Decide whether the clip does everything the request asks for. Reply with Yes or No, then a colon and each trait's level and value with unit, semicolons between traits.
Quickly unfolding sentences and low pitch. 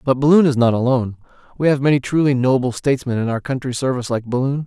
Yes: fast, 220 wpm; low, 130 Hz